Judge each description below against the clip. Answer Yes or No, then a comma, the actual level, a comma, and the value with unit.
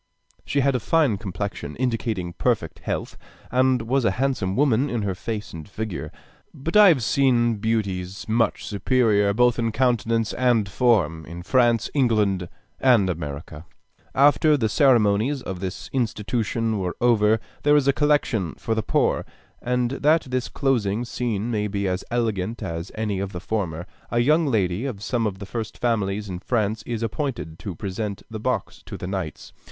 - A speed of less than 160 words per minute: No, average, 170 wpm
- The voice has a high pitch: No, low, 110 Hz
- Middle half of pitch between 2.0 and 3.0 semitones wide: No, average, 4.2 semitones